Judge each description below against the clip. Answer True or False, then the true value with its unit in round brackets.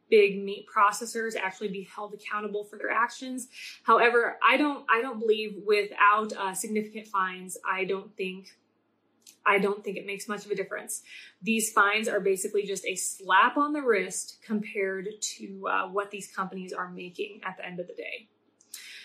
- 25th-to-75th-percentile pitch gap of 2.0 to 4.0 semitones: True (2.8 semitones)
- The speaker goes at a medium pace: True (175 wpm)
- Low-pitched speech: False (210 Hz)